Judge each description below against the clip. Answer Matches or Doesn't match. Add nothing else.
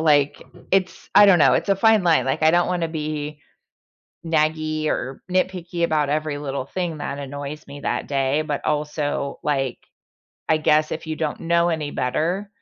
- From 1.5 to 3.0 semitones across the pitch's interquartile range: Matches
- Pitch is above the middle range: Doesn't match